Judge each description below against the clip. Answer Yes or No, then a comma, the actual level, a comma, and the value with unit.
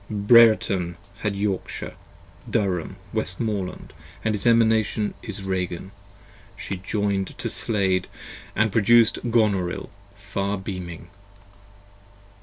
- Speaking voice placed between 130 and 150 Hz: No, low, 100 Hz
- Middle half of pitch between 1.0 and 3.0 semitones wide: Yes, narrow, 2.6 semitones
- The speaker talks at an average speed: No, slow, 90 wpm